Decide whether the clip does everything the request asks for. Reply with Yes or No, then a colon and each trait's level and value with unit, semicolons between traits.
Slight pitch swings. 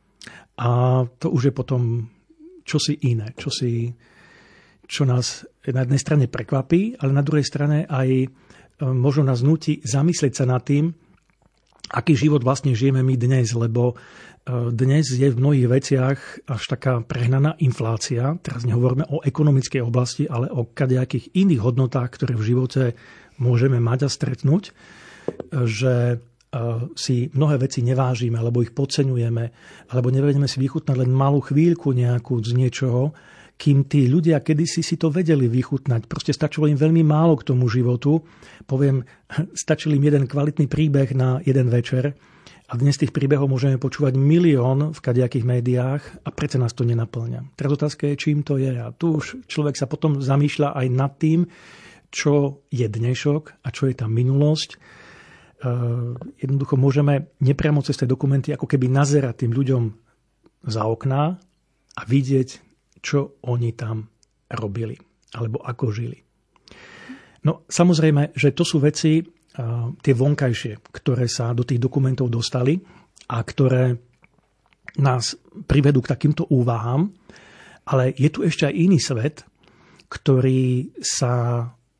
No: average, 3.1 semitones